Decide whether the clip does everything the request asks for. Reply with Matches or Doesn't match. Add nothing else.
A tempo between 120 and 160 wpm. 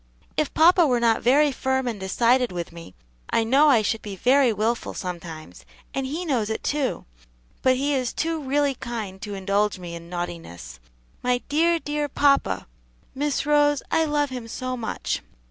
Doesn't match